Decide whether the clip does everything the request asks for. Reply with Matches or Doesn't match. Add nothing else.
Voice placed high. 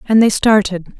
Matches